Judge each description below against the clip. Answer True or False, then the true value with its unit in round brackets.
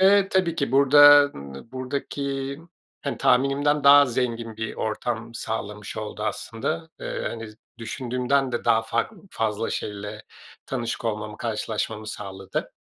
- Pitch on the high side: False (120 Hz)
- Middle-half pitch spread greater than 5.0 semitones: False (4.3 semitones)